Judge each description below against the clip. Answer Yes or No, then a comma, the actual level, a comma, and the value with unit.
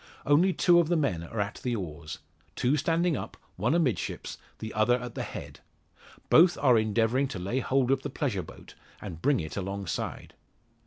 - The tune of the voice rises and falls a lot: Yes, wide, 6.4 semitones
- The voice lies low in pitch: Yes, low, 125 Hz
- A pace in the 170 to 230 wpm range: Yes, average, 180 wpm